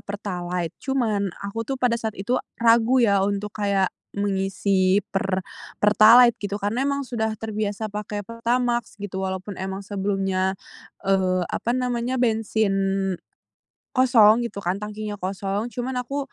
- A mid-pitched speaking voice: No, high, 210 Hz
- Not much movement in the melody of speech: No, average, 3.2 semitones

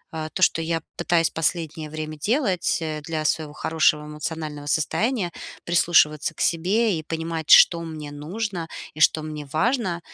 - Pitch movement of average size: No, narrow, 2.1 semitones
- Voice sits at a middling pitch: Yes, medium, 160 Hz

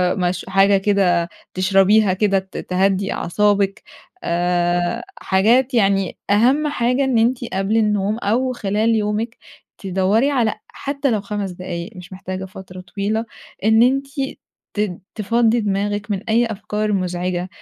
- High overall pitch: Yes, high, 205 Hz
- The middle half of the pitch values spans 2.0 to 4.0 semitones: Yes, average, 3.0 semitones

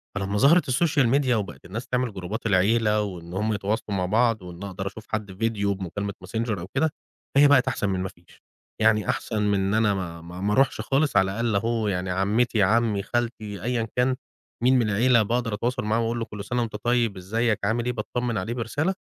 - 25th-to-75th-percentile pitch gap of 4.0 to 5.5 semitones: No, average, 3.4 semitones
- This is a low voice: Yes, low, 110 Hz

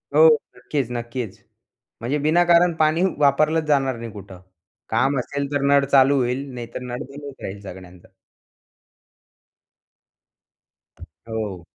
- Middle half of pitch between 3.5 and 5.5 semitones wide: Yes, average, 3.8 semitones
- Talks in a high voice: No, low, 135 Hz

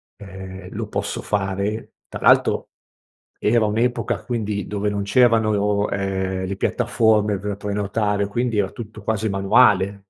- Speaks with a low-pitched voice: Yes, low, 105 Hz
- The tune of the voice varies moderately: No, narrow, 1.9 semitones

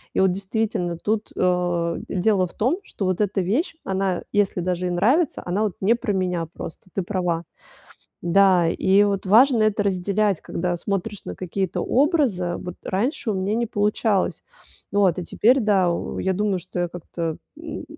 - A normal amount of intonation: Yes, average, 3.0 semitones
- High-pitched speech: Yes, high, 195 Hz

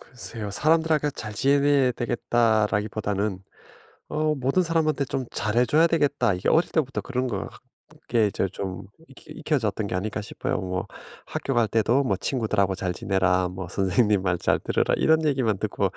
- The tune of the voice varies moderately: No, wide, 5.8 semitones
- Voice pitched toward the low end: Yes, low, 115 Hz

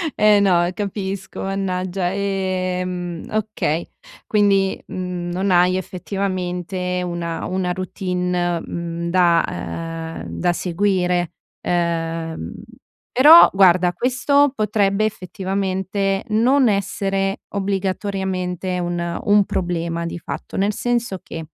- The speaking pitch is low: No, medium, 185 Hz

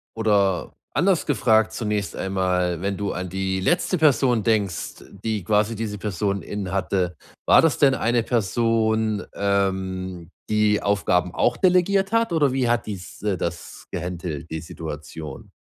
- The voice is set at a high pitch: No, low, 100 Hz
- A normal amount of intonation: Yes, average, 3.7 semitones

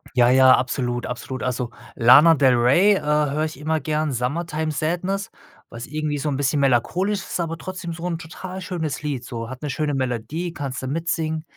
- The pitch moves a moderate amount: Yes, average, 4.2 semitones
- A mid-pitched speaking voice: Yes, medium, 150 Hz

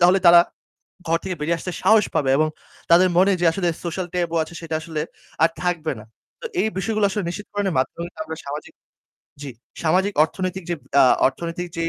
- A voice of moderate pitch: Yes, medium, 175 Hz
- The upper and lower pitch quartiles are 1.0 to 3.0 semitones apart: Yes, average, 2.7 semitones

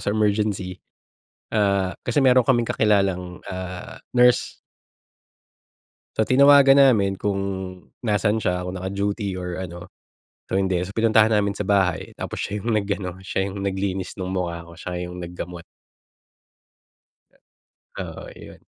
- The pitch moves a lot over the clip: No, narrow, 2.6 semitones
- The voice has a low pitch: Yes, low, 100 Hz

